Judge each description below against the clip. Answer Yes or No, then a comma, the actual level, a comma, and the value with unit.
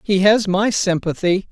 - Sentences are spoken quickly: No, average, 160 wpm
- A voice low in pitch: No, high, 195 Hz